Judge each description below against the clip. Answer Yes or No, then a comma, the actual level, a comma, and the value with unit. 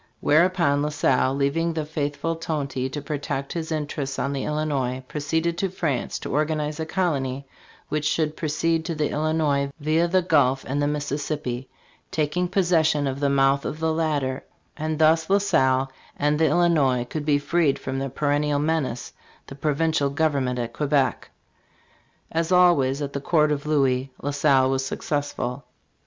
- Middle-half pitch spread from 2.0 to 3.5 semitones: Yes, narrow, 2.6 semitones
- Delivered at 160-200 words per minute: Yes, average, 165 wpm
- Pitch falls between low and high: Yes, medium, 150 Hz